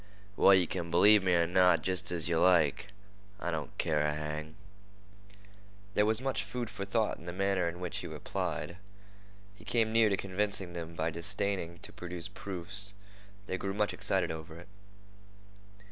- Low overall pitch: Yes, very low, 90 Hz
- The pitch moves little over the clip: No, average, 3.2 semitones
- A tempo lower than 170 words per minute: No, average, 175 wpm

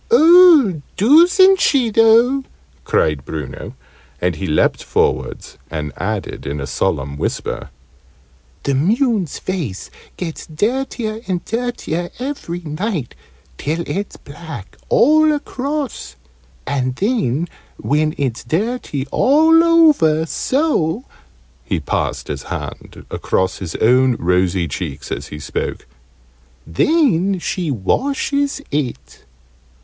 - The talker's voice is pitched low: No, medium, 175 Hz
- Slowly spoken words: Yes, slow, 110 wpm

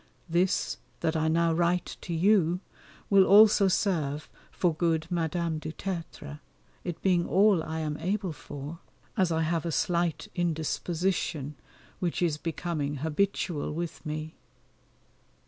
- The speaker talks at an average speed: No, slow, 130 wpm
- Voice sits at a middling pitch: Yes, medium, 170 Hz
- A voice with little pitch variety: Yes, narrow, 2.3 semitones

